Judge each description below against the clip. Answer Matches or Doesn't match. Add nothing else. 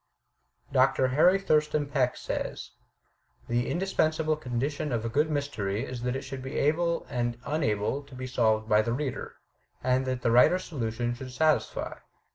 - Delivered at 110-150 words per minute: Doesn't match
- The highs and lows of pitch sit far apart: Doesn't match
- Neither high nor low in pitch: Doesn't match